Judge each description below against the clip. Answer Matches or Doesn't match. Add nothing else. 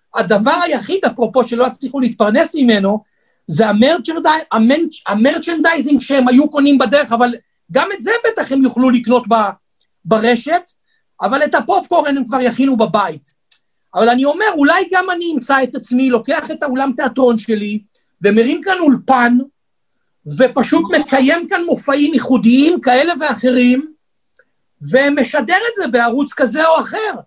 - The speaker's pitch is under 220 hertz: Doesn't match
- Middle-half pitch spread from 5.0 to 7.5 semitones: Doesn't match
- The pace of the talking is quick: Doesn't match